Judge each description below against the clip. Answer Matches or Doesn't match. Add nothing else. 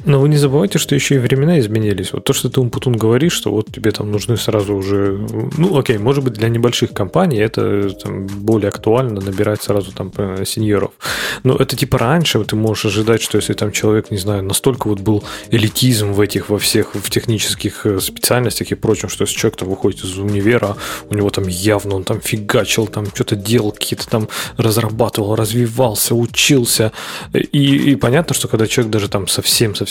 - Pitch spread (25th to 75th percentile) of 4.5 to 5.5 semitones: Doesn't match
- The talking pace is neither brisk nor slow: Doesn't match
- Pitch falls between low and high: Doesn't match